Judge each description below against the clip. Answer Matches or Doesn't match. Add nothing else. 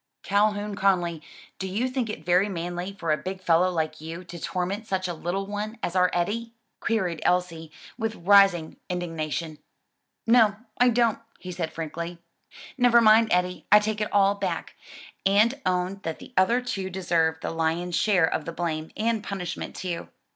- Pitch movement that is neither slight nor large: Matches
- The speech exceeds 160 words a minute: Matches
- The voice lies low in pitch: Doesn't match